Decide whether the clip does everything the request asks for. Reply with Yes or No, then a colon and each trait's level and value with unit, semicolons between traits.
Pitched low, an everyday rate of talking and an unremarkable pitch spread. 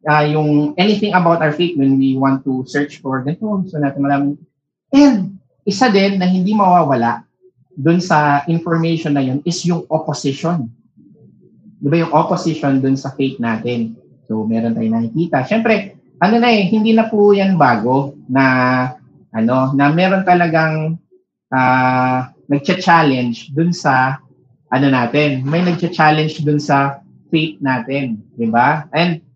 No: medium, 150 Hz; average, 145 wpm; average, 4.7 semitones